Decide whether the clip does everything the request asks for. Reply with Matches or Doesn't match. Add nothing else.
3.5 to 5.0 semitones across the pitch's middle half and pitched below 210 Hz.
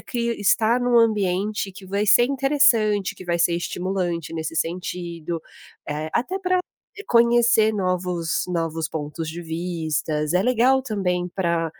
Doesn't match